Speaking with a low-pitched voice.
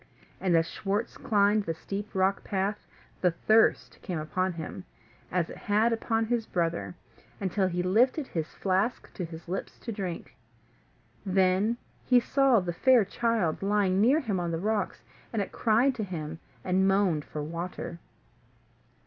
No: high, 195 Hz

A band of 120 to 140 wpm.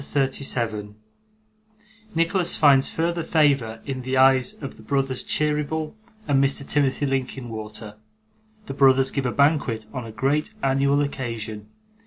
Yes: slow, 135 wpm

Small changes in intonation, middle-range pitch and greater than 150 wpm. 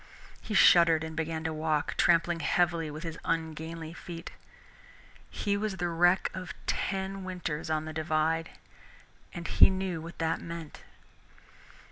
No: narrow, 1.8 semitones; medium, 165 Hz; average, 140 wpm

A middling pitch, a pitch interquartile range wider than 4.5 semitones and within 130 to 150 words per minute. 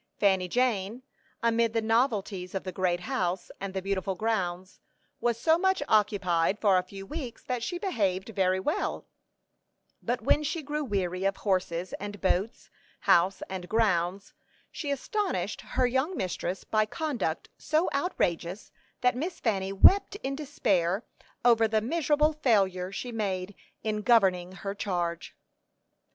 No: high, 205 Hz; average, 5.0 semitones; average, 145 wpm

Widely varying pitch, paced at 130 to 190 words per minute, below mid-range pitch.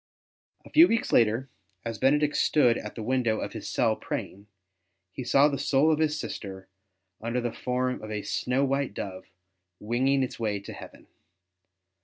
No: average, 4.1 semitones; average, 170 wpm; low, 125 Hz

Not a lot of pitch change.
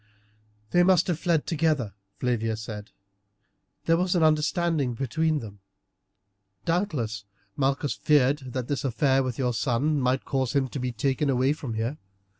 No: average, 4.1 semitones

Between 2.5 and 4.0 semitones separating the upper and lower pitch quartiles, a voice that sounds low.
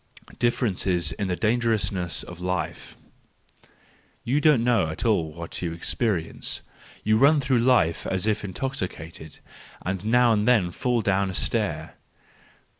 No: average, 5.2 semitones; low, 100 Hz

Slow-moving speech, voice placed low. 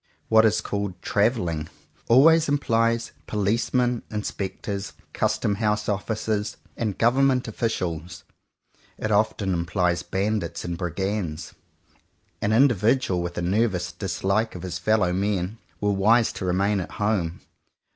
Yes: slow, 130 wpm; low, 105 Hz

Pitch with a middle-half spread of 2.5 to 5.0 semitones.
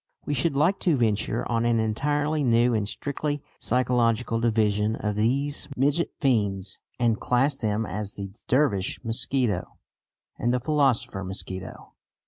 Yes: average, 4.5 semitones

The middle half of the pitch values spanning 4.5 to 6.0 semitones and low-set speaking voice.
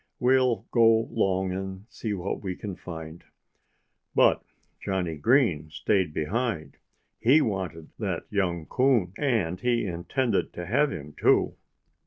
Yes: average, 5.3 semitones; very low, 95 Hz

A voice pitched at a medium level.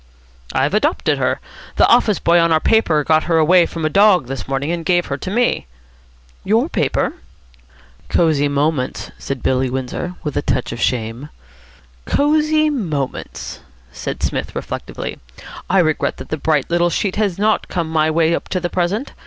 Yes: medium, 165 Hz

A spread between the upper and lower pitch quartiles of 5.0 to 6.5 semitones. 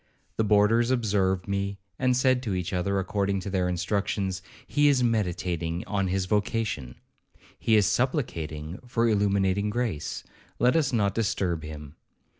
No: average, 3.9 semitones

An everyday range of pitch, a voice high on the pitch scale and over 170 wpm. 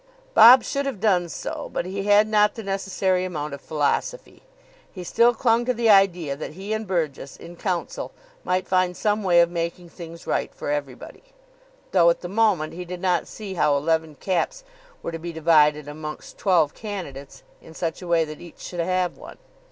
No: average, 3.9 semitones; medium, 180 Hz; average, 190 wpm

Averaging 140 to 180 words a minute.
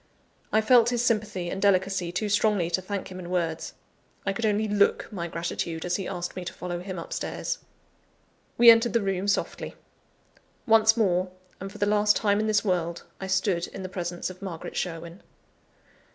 No: average, 190 wpm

